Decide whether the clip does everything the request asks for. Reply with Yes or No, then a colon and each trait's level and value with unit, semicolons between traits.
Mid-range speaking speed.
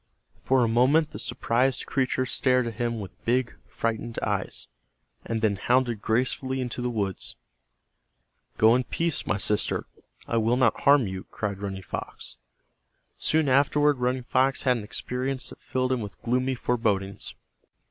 Yes: average, 155 wpm